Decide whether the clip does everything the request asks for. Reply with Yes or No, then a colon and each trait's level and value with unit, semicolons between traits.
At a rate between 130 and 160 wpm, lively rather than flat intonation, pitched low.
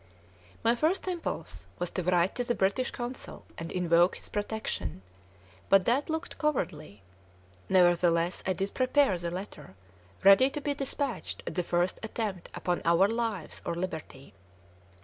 No: average, 150 wpm; wide, 5.9 semitones; high, 190 Hz